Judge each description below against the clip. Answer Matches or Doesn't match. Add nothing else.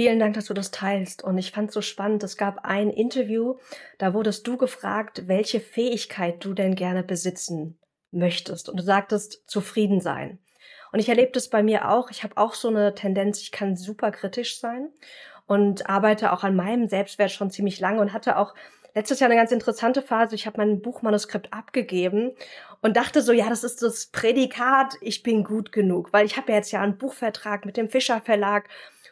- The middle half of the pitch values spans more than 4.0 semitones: Doesn't match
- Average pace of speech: Doesn't match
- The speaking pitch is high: Matches